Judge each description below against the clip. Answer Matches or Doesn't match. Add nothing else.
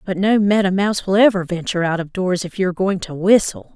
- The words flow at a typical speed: Doesn't match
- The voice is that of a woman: Matches